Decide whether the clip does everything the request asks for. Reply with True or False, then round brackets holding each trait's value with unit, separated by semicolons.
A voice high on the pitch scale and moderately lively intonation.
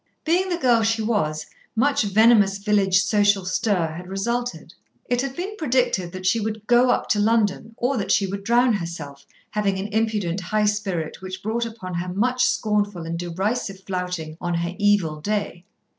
True (205 Hz; 4.0 semitones)